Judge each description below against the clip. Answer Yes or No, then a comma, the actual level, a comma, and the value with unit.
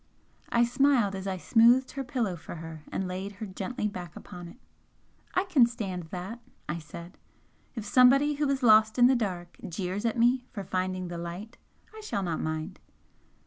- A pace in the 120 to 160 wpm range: No, average, 185 wpm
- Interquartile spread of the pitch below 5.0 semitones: No, average, 5.3 semitones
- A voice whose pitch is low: No, high, 200 Hz